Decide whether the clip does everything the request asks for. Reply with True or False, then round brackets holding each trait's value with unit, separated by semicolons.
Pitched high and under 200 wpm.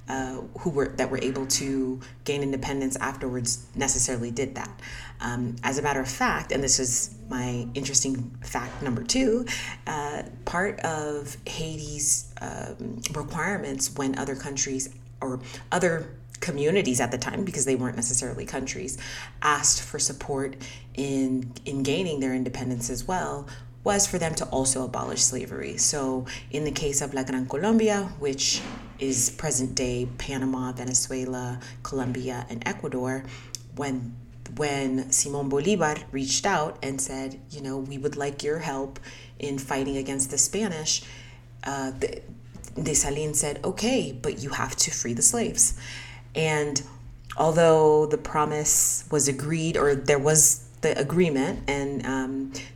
False (135 Hz; 145 wpm)